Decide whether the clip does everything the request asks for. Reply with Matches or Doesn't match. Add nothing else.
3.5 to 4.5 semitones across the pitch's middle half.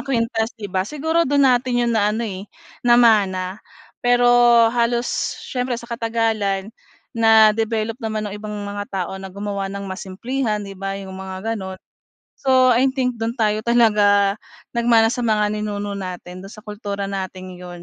Doesn't match